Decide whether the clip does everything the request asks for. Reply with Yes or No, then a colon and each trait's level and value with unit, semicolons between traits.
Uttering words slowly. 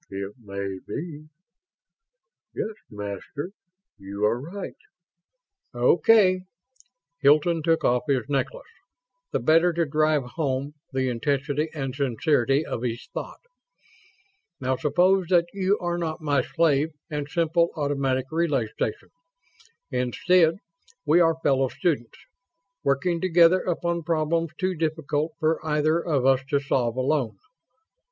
Yes: slow, 120 wpm